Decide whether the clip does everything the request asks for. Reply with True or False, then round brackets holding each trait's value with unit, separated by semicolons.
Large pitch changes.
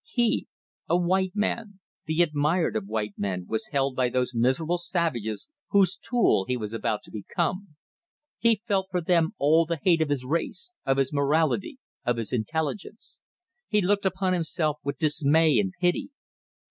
True (6.3 semitones)